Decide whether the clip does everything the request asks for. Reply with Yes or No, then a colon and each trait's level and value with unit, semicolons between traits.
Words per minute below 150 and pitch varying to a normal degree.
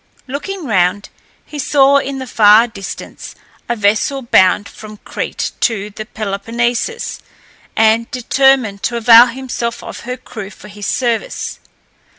Yes: slow, 135 wpm; average, 3.8 semitones